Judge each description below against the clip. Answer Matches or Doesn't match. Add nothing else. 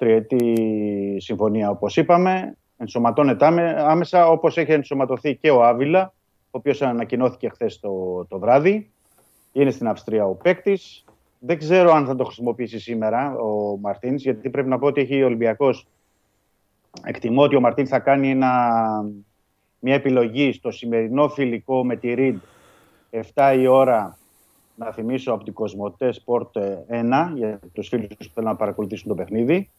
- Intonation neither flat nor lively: Matches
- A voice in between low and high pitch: Doesn't match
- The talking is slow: Doesn't match